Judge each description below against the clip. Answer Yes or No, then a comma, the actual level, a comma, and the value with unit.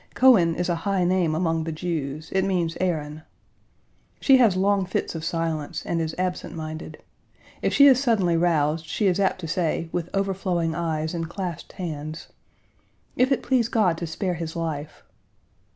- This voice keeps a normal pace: Yes, average, 170 wpm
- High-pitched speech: No, medium, 170 Hz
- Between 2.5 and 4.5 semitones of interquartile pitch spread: Yes, average, 2.8 semitones